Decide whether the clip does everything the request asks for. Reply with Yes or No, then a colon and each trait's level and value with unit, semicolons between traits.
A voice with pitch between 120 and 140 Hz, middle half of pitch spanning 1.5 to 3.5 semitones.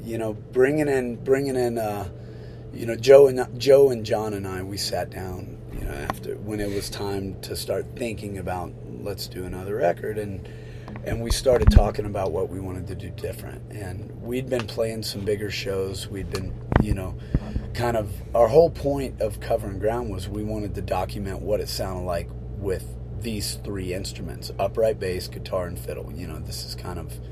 No: low, 105 Hz; average, 3.1 semitones